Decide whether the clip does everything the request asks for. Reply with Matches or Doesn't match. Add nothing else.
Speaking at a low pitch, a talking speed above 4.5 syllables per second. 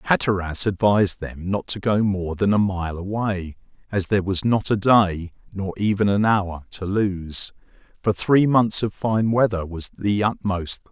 Doesn't match